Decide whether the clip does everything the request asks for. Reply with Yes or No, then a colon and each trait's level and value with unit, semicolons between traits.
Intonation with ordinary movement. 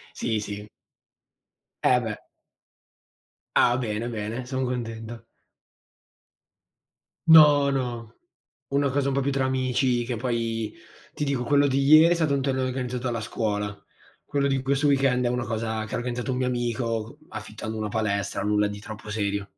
Yes: average, 3.3 semitones